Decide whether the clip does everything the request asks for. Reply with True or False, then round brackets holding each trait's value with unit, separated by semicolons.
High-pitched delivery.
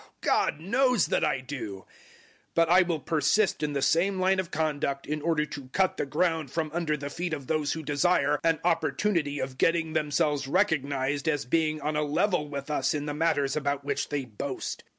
False (150 Hz)